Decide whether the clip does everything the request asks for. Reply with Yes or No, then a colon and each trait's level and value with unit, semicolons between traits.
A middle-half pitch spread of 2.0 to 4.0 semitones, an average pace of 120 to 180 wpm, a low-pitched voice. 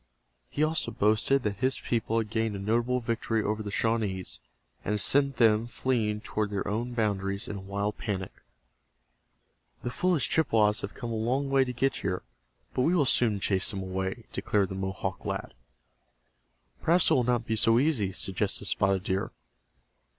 Yes: average, 3.6 semitones; average, 175 wpm; low, 110 Hz